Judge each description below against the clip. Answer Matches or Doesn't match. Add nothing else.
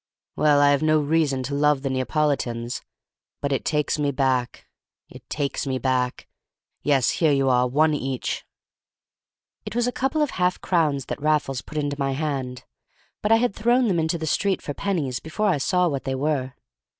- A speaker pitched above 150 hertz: Doesn't match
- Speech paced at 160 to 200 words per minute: Matches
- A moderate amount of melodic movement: Matches